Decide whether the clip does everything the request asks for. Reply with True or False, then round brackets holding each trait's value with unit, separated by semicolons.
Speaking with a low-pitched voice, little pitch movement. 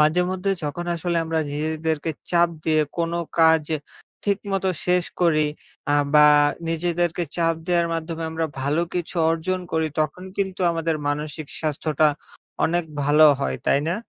False (165 Hz; 2.1 semitones)